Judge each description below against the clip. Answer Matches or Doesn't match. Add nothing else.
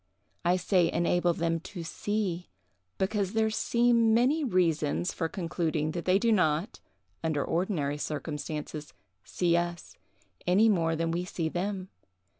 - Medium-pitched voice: Matches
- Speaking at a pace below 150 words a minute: Matches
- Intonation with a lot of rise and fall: Doesn't match